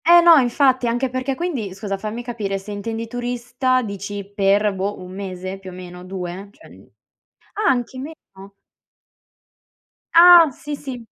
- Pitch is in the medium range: No, high, 225 Hz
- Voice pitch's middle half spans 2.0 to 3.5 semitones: No, average, 4.9 semitones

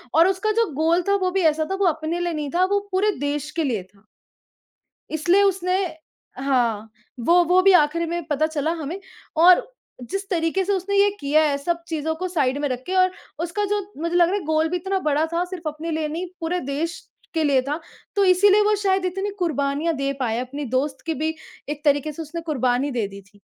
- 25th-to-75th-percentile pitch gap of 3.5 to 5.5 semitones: Yes, average, 4.1 semitones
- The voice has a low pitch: No, very high, 325 Hz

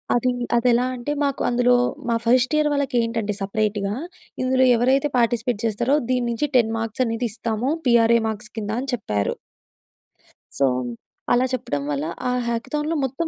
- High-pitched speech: Yes, high, 235 Hz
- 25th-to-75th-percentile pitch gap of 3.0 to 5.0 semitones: No, narrow, 2.5 semitones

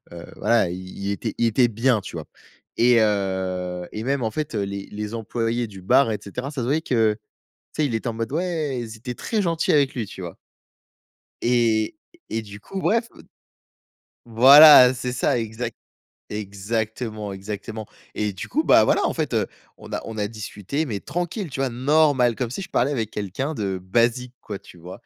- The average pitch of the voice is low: Yes, low, 115 Hz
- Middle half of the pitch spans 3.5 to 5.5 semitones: Yes, average, 4.1 semitones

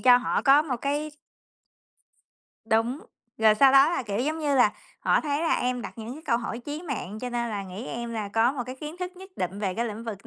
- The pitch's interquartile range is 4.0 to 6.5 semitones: Yes, average, 4.6 semitones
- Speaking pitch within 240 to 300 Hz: Yes, high, 245 Hz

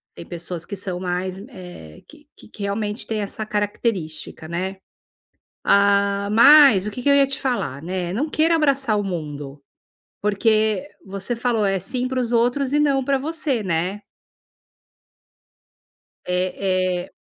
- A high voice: Yes, high, 200 Hz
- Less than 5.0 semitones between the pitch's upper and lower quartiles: No, wide, 5.4 semitones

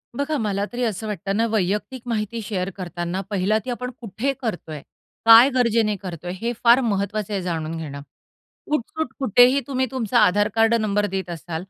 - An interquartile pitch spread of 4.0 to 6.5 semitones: Yes, average, 4.3 semitones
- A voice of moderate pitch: No, high, 210 Hz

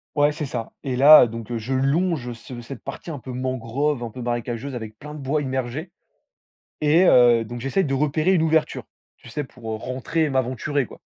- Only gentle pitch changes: No, average, 3.7 semitones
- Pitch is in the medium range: No, low, 130 Hz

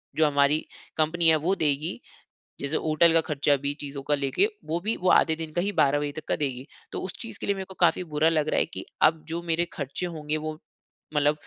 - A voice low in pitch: No, medium, 155 Hz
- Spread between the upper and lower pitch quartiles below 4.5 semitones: Yes, narrow, 2.6 semitones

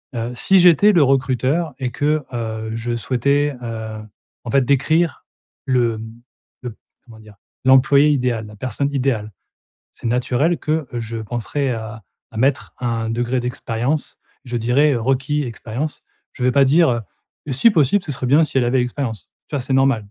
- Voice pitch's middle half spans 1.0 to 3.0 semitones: No, average, 3.6 semitones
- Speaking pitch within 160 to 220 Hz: No, low, 125 Hz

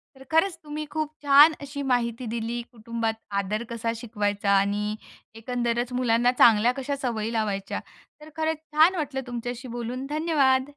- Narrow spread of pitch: No, average, 4.0 semitones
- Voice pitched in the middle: No, high, 245 Hz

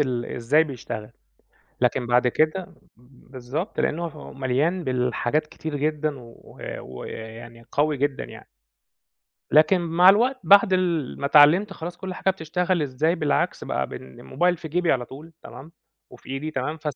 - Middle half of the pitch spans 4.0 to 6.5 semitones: Yes, average, 5.2 semitones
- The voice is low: No, medium, 150 Hz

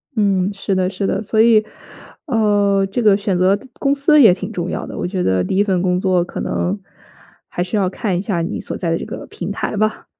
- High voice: Yes, high, 195 Hz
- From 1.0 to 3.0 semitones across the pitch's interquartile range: Yes, average, 2.7 semitones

